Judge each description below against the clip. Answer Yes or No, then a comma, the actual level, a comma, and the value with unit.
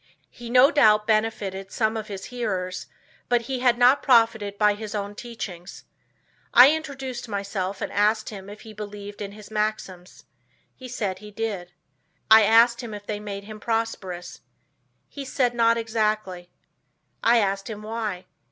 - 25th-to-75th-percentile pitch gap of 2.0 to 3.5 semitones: Yes, narrow, 2.5 semitones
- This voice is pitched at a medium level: No, high, 215 Hz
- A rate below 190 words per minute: Yes, average, 160 wpm